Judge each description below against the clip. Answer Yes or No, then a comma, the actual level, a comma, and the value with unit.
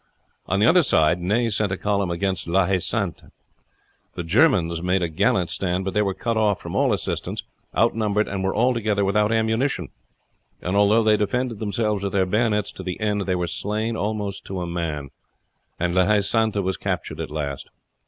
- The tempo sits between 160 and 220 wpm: Yes, average, 195 wpm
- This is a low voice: Yes, low, 100 Hz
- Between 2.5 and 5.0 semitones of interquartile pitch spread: Yes, average, 3.0 semitones